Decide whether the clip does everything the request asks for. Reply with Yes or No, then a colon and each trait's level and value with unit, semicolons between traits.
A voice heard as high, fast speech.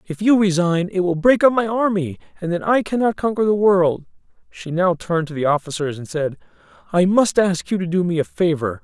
No: medium, 175 Hz; fast, 225 wpm